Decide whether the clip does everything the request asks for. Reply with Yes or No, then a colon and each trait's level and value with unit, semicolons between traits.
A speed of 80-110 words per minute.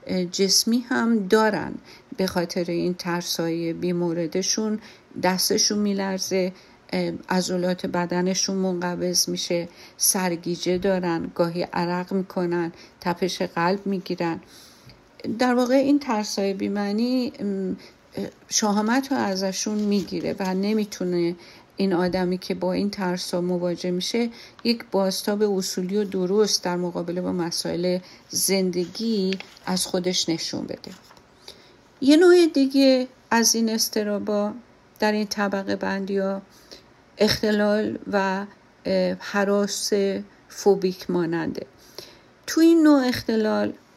Yes: slow, 105 wpm